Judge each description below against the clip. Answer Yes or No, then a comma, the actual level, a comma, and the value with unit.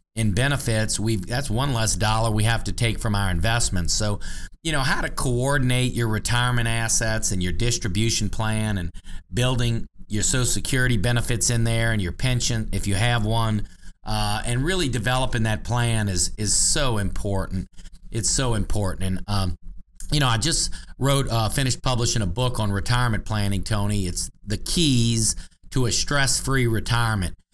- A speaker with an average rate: Yes, average, 170 wpm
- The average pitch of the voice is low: Yes, low, 110 Hz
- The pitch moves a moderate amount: Yes, average, 3.6 semitones